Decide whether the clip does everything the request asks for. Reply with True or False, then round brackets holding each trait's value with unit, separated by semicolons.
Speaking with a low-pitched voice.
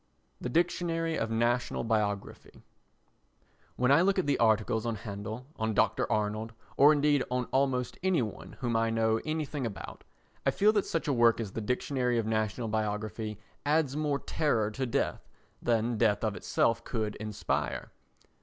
True (115 Hz)